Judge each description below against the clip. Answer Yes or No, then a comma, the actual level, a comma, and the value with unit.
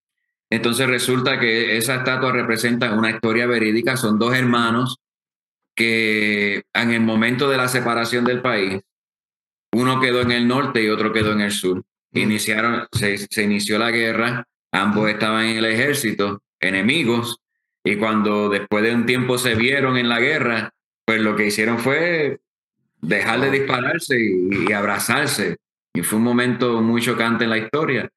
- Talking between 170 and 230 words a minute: No, average, 160 wpm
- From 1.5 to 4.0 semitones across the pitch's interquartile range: Yes, narrow, 2.4 semitones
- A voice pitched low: Yes, low, 115 Hz